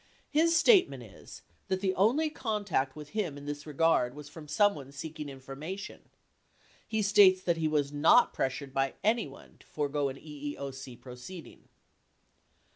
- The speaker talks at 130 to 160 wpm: Yes, average, 150 wpm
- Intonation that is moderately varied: No, wide, 6.3 semitones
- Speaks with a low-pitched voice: No, medium, 150 Hz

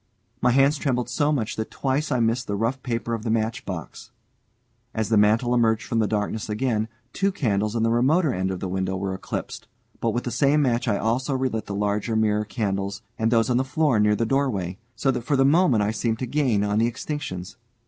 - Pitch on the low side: Yes, low, 115 Hz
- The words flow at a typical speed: No, fast, 220 wpm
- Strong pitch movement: No, average, 3.7 semitones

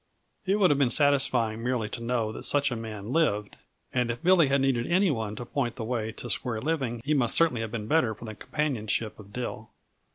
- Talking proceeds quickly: Yes, fast, 225 wpm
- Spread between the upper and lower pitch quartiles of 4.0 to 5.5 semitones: Yes, average, 4.3 semitones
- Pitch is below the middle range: Yes, low, 120 Hz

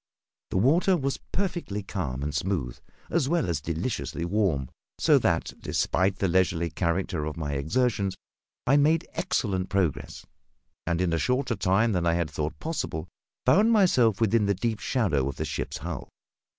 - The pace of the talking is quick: No, average, 165 wpm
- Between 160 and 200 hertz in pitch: No, very low, 95 Hz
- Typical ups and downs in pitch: No, wide, 7.2 semitones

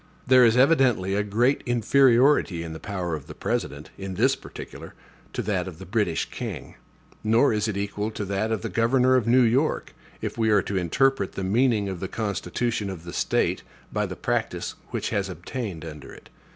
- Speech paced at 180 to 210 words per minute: Yes, average, 195 wpm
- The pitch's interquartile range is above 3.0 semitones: Yes, average, 4.5 semitones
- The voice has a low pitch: Yes, low, 105 Hz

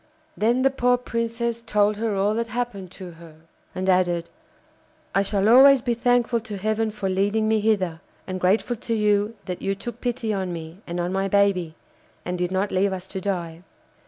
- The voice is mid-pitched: No, high, 205 Hz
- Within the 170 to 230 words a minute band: Yes, average, 190 wpm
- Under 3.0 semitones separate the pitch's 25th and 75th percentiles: No, average, 3.7 semitones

